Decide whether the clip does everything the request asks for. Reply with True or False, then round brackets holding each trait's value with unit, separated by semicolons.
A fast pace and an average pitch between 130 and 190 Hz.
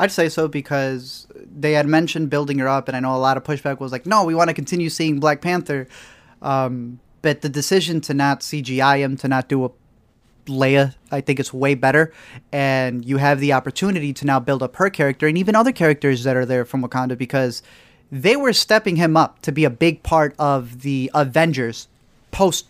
True (210 wpm; 140 Hz)